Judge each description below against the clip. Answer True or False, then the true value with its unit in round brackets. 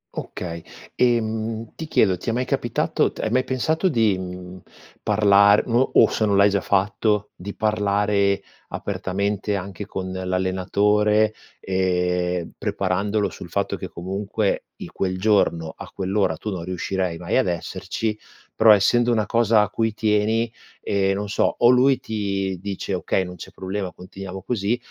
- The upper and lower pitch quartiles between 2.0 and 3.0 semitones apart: True (2.6 semitones)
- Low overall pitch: True (100 Hz)